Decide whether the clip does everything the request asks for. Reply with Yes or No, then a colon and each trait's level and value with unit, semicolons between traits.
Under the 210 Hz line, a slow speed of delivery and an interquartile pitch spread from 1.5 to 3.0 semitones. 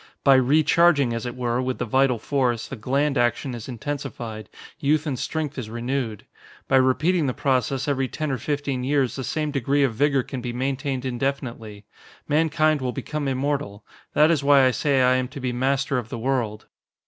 No: low, 135 Hz; average, 190 wpm; average, 2.7 semitones